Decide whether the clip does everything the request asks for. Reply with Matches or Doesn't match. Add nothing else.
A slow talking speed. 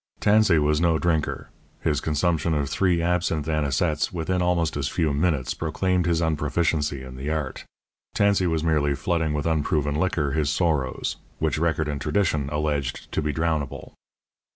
Doesn't match